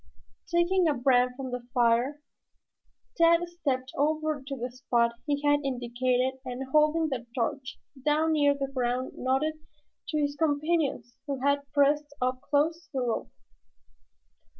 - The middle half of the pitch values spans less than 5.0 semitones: Yes, average, 3.2 semitones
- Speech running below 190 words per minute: Yes, average, 145 wpm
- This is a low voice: No, very high, 280 Hz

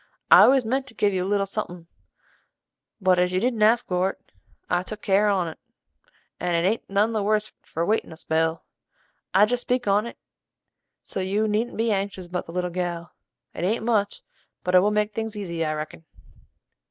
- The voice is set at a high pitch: Yes, high, 200 Hz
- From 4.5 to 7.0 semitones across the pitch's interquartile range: No, average, 3.3 semitones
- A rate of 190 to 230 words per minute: Yes, average, 195 wpm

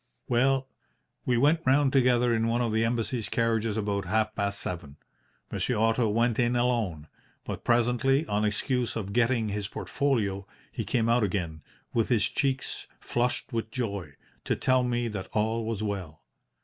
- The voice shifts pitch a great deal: No, average, 3.0 semitones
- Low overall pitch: Yes, low, 115 Hz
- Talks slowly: No, average, 160 wpm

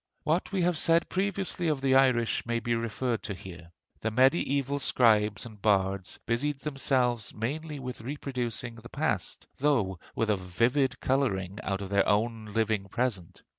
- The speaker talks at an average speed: Yes, average, 160 wpm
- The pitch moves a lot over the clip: No, average, 4.7 semitones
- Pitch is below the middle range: Yes, low, 120 Hz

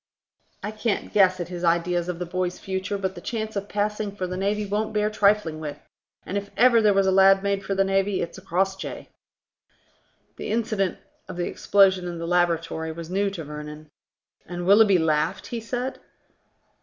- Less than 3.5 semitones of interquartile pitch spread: Yes, average, 2.7 semitones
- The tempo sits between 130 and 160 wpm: No, average, 185 wpm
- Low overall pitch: No, high, 190 Hz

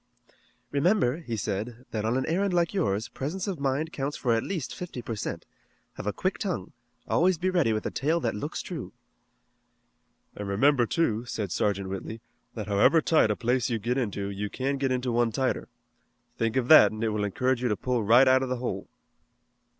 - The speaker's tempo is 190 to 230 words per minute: Yes, fast, 205 wpm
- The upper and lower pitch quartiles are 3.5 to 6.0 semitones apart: Yes, average, 4.6 semitones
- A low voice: Yes, low, 125 Hz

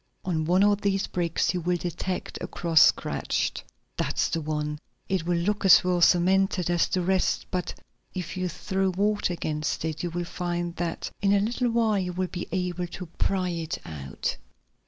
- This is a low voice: No, medium, 180 Hz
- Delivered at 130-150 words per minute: No, average, 185 wpm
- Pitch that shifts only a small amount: Yes, narrow, 2.1 semitones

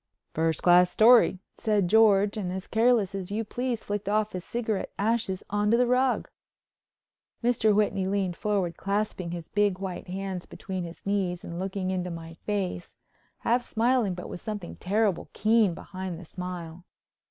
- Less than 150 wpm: No, average, 160 wpm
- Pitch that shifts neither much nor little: Yes, average, 3.2 semitones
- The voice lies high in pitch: Yes, high, 195 Hz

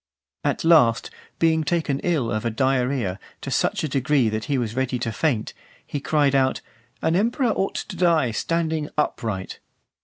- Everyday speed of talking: Yes, average, 165 wpm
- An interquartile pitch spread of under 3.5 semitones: No, average, 5.3 semitones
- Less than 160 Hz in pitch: Yes, medium, 140 Hz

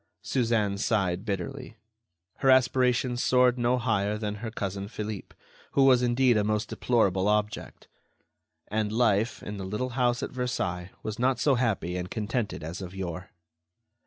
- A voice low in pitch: Yes, low, 110 Hz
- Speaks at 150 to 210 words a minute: Yes, average, 155 wpm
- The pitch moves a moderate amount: Yes, average, 3.9 semitones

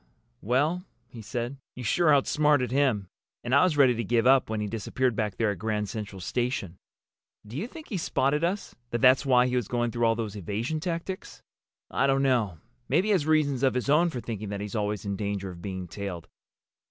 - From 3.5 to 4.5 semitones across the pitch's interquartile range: No, average, 5.1 semitones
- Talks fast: Yes, fast, 210 wpm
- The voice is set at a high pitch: No, low, 120 Hz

